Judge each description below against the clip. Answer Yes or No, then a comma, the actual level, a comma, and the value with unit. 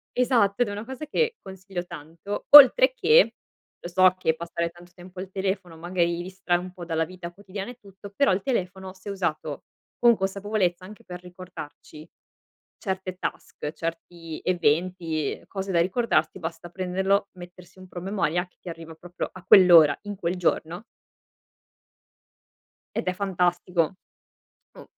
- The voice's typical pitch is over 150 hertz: Yes, medium, 185 Hz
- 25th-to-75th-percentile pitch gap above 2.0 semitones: Yes, narrow, 2.4 semitones